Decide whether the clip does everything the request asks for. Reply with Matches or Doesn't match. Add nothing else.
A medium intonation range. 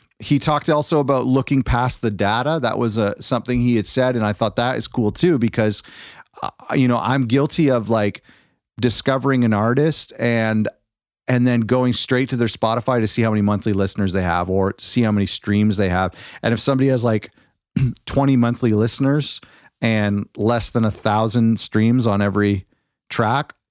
Matches